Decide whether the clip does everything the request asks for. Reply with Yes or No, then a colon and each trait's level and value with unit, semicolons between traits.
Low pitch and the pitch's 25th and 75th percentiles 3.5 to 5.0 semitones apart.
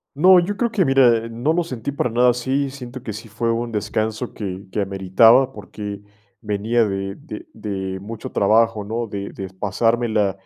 Yes: low, 115 Hz; average, 3.8 semitones